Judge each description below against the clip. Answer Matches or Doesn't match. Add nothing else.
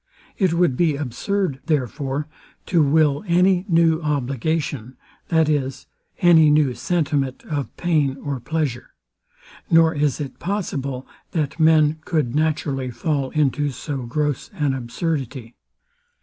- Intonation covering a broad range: Doesn't match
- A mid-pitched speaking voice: Matches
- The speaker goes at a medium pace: Doesn't match